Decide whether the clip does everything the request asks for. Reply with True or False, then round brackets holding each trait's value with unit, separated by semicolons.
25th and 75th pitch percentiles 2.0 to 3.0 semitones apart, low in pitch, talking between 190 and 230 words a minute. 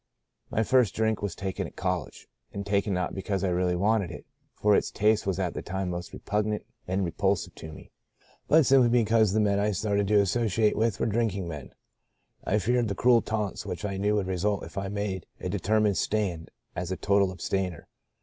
True (2.5 semitones; 100 Hz; 200 wpm)